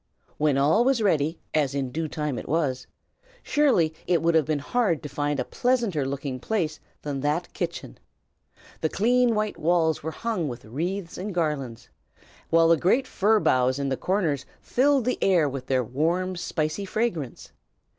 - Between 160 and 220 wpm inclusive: Yes, average, 170 wpm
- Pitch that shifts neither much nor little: No, wide, 5.7 semitones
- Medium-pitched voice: Yes, medium, 160 Hz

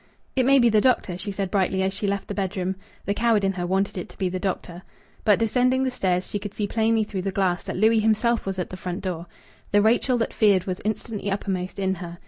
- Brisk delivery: Yes, fast, 250 wpm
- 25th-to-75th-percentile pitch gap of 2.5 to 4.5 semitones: Yes, average, 2.8 semitones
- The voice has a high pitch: Yes, high, 200 Hz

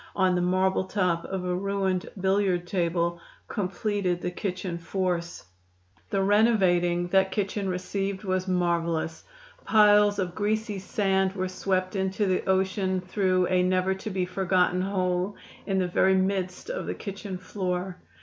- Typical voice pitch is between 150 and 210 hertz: Yes, medium, 185 Hz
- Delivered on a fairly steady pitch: Yes, narrow, 1.5 semitones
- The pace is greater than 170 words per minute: No, average, 145 wpm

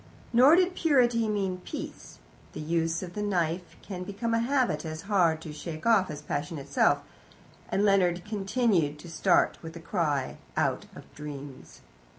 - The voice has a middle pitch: Yes, medium, 180 Hz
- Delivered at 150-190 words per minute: Yes, average, 160 wpm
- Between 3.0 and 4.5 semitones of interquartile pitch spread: No, average, 4.9 semitones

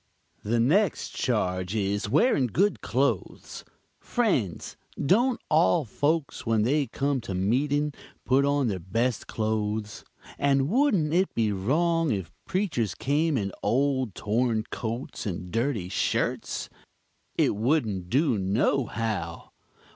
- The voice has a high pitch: No, low, 125 Hz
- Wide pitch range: Yes, wide, 6.1 semitones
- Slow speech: Yes, slow, 125 wpm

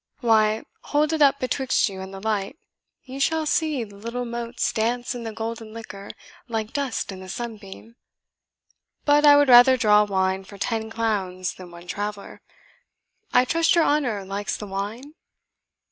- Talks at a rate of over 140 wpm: Yes, average, 165 wpm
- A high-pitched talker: Yes, high, 225 Hz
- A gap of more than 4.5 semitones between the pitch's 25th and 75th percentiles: No, average, 4.2 semitones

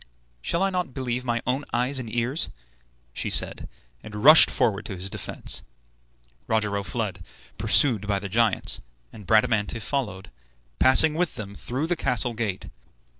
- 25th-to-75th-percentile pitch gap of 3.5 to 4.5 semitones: Yes, average, 4.2 semitones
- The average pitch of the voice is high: No, low, 115 Hz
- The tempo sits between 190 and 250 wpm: No, average, 150 wpm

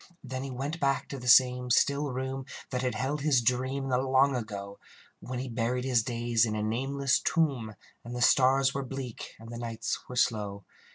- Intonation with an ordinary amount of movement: No, narrow, 2.3 semitones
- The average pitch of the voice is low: Yes, low, 125 Hz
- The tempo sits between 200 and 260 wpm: Yes, fast, 205 wpm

